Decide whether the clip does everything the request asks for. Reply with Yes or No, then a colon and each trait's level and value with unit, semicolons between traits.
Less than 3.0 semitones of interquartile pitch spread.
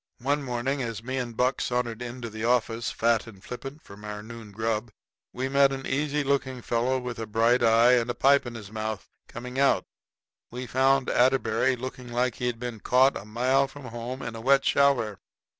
Yes: narrow, 2.6 semitones